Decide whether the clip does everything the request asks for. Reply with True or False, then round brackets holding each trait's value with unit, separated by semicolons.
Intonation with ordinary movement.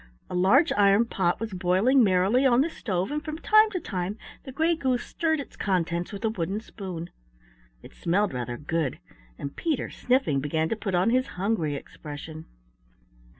False (6.9 semitones)